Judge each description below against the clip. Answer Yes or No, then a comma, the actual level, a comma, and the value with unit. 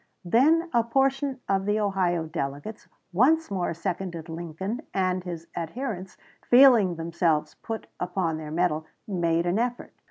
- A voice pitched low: No, medium, 185 Hz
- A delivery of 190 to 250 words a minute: No, slow, 135 wpm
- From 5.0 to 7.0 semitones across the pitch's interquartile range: Yes, wide, 5.6 semitones